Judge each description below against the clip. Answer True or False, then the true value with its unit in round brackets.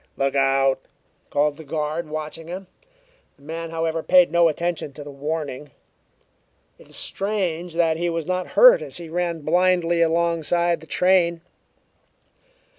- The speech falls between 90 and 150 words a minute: True (145 wpm)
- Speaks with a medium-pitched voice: True (165 Hz)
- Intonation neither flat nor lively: False (2.2 semitones)